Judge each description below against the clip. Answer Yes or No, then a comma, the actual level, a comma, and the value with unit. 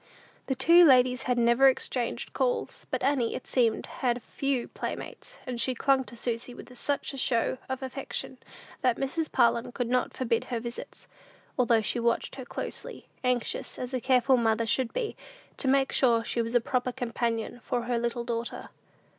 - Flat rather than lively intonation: Yes, narrow, 2.0 semitones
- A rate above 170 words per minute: Yes, average, 180 wpm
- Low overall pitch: No, very high, 250 Hz